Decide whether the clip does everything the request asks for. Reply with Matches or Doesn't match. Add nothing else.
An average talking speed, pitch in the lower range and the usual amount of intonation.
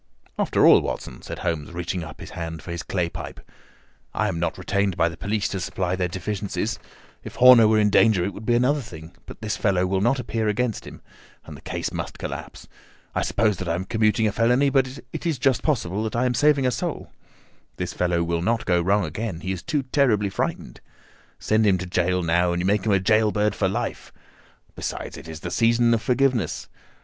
Doesn't match